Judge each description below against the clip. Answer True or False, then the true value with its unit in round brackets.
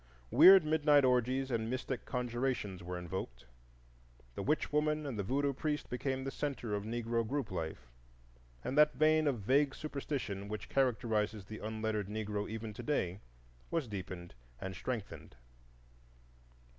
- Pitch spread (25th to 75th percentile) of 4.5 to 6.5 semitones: True (5.1 semitones)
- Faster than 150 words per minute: False (145 wpm)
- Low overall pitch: True (120 Hz)